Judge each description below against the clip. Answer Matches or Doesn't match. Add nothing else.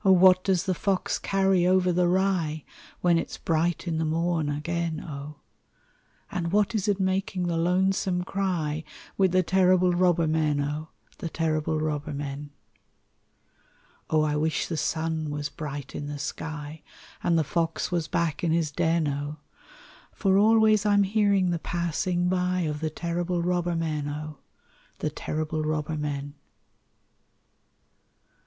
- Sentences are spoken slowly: Doesn't match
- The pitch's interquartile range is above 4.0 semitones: Doesn't match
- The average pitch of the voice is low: Doesn't match